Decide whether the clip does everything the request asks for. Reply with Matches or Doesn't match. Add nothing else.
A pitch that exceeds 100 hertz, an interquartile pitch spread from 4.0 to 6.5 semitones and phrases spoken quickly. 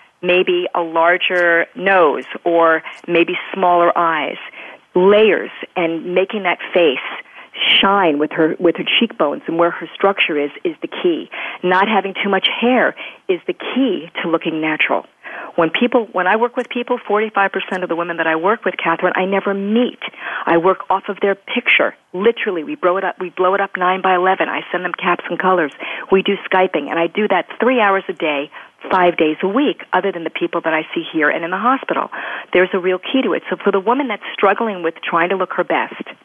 Doesn't match